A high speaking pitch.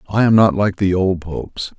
No: very low, 95 Hz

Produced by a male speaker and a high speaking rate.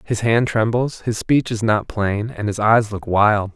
Yes: male; fast, 220 wpm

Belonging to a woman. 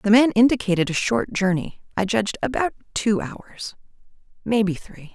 Yes: female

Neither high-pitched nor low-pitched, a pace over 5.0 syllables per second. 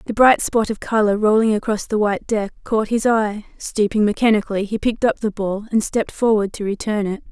No: high, 215 Hz; 5.7 syllables/s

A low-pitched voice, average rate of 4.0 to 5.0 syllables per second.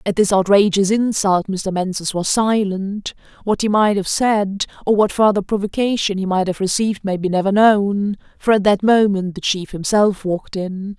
No: high, 200 Hz; 4.8 syllables/s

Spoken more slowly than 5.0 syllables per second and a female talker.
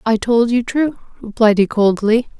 Yes: 4.5 syllables/s; female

